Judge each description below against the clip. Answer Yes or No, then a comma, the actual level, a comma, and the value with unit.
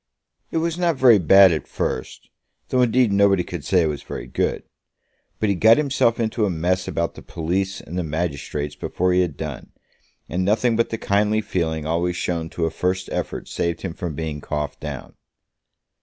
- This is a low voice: Yes, very low, 90 Hz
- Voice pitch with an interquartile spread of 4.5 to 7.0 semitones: Yes, average, 4.8 semitones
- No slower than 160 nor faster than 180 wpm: No, average, 190 wpm